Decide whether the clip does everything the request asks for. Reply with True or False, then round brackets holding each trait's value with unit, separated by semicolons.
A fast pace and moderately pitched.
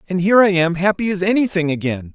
True (225 wpm; 180 Hz)